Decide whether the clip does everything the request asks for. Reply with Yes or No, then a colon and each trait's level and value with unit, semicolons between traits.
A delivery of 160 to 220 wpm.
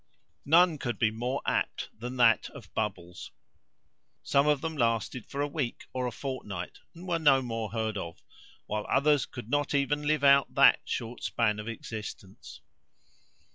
Yes: average, 165 wpm